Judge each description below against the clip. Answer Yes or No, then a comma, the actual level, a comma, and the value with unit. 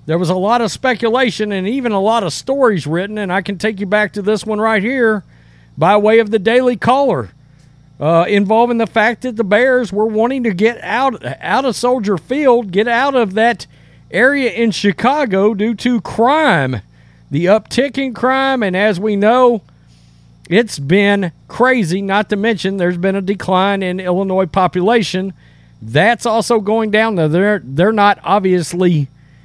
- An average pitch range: Yes, average, 4.3 semitones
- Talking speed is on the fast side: No, average, 175 wpm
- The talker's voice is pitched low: No, high, 210 Hz